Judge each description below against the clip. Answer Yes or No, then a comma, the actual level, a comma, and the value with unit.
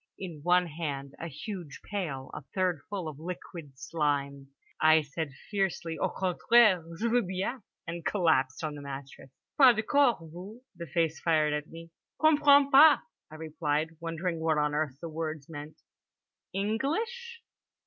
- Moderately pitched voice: Yes, medium, 165 Hz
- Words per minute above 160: No, average, 155 wpm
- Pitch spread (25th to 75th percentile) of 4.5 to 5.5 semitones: Yes, average, 5.0 semitones